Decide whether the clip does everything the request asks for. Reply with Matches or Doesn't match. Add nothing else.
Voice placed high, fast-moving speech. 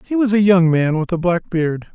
Doesn't match